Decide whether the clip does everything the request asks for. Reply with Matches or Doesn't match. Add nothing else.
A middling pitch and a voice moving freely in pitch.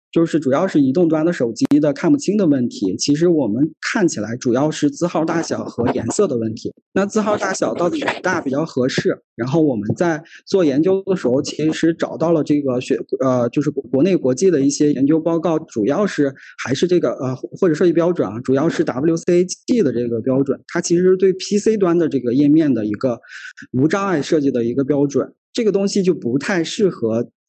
Matches